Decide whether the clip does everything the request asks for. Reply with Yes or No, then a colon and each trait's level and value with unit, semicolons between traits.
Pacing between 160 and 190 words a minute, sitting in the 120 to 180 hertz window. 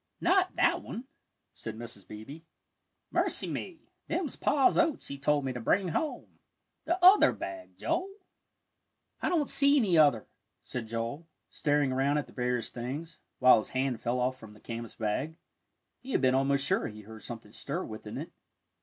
Yes: average, 170 wpm; low, 135 Hz